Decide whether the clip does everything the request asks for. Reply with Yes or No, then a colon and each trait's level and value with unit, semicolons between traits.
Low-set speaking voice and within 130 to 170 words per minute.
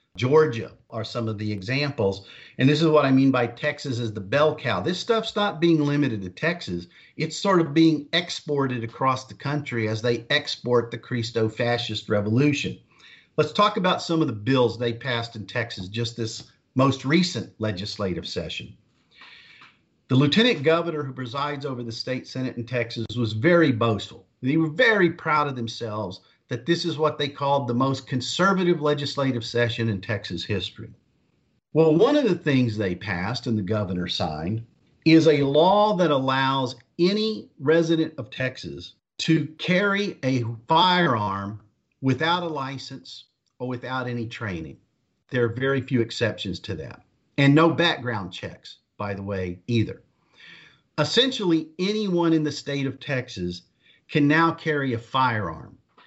Yes: low, 130 Hz; average, 160 wpm